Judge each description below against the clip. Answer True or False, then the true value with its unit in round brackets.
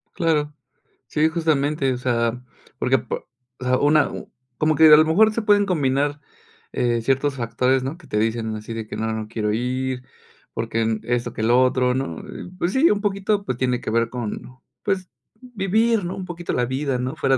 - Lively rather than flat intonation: True (5.8 semitones)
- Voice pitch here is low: True (130 Hz)